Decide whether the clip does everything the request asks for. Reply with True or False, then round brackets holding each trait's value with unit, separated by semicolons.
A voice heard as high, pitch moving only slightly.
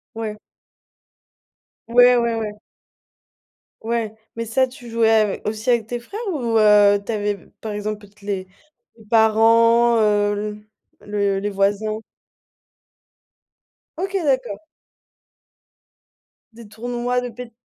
True (220 Hz; 2.3 semitones)